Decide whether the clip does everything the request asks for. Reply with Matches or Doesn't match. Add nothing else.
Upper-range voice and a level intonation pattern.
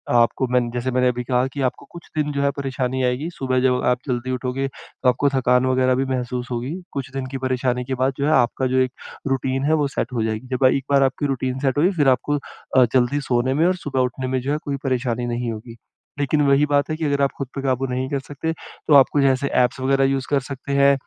Doesn't match